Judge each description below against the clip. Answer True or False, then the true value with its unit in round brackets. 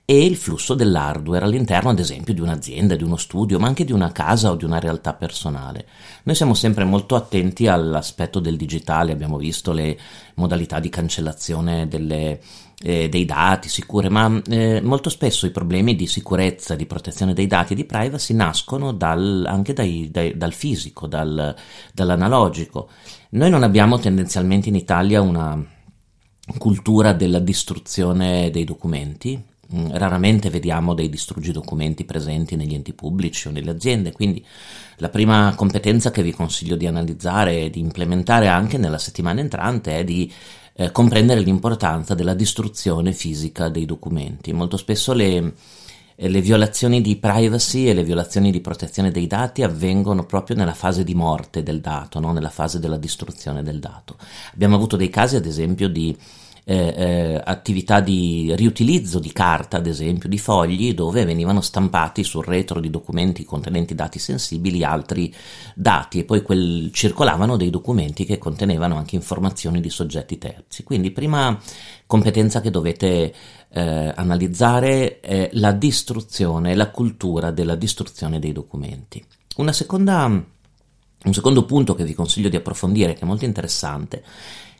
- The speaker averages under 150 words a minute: False (155 wpm)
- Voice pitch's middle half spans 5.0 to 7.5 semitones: False (4.2 semitones)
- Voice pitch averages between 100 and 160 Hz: False (90 Hz)